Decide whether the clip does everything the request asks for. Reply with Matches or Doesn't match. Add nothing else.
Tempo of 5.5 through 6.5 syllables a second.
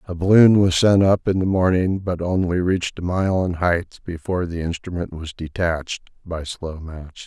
Doesn't match